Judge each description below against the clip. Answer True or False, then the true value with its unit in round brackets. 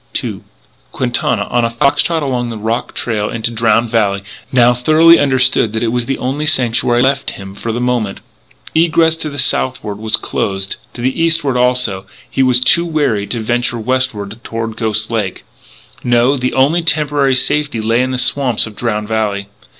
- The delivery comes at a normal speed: True (180 wpm)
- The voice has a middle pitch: False (120 Hz)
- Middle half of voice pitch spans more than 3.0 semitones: True (3.5 semitones)